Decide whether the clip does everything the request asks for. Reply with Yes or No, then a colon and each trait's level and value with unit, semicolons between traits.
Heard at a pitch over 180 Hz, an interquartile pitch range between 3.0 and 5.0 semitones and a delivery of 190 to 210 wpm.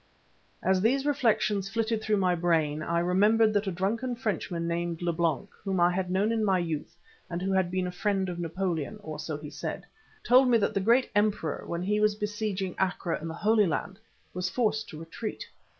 Yes: high, 190 Hz; average, 3.7 semitones; average, 200 wpm